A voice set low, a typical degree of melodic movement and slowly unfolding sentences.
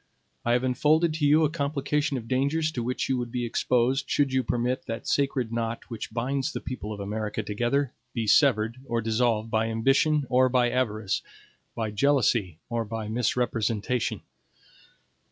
No: low, 125 Hz; average, 3.4 semitones; average, 165 wpm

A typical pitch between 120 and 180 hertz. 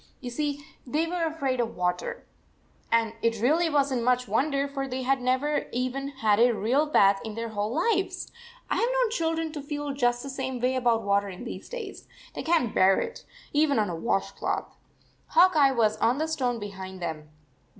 No: very high, 255 Hz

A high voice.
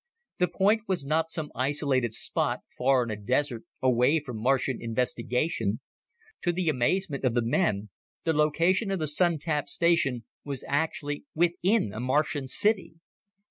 No: medium, 145 Hz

